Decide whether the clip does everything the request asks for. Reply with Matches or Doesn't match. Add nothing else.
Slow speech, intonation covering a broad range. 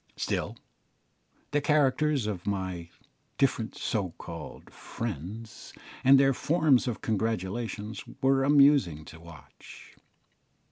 Matches